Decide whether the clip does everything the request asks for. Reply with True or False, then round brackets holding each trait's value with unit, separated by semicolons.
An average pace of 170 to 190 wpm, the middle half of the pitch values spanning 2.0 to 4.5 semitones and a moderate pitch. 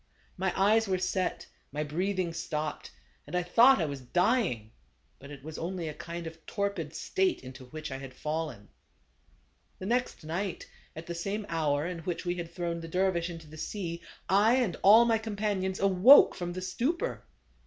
True (185 wpm; 4.1 semitones; 175 Hz)